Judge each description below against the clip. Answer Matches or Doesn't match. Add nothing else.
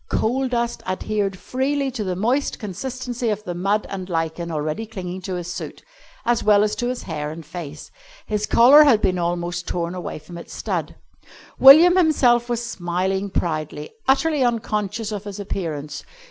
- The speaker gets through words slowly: Doesn't match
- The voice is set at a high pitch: Matches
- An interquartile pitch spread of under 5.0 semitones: Doesn't match